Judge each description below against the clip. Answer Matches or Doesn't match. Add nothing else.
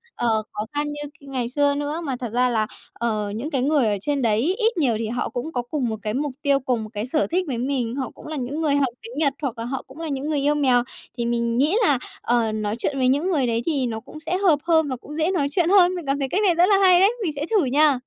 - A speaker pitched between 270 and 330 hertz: Matches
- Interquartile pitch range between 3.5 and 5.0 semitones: Matches